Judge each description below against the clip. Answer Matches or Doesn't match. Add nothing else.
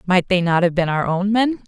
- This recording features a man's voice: Doesn't match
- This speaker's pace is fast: Matches